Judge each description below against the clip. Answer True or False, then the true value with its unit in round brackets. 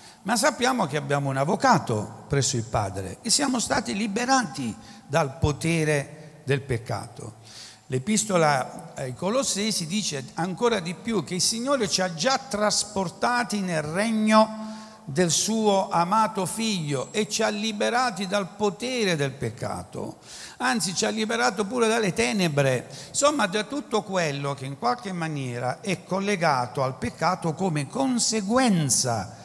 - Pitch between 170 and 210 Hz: True (190 Hz)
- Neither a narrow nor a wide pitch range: False (7.5 semitones)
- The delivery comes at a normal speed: True (135 wpm)